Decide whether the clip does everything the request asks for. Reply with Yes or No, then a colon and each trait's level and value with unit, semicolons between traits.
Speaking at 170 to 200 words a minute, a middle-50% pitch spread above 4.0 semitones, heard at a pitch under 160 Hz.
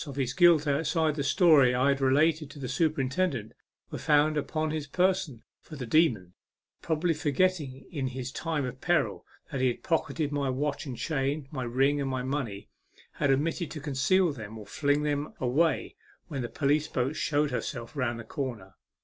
No: average, 185 wpm; average, 3.2 semitones; medium, 140 Hz